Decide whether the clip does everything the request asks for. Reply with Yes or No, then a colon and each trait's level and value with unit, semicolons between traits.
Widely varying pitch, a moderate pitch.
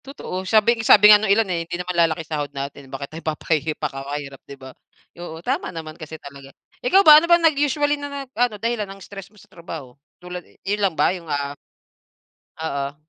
Yes: wide, 7.2 semitones; medium, 175 Hz